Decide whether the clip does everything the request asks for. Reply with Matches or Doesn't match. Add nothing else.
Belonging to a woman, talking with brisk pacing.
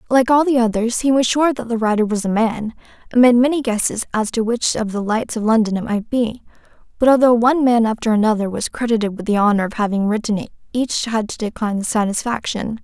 Matches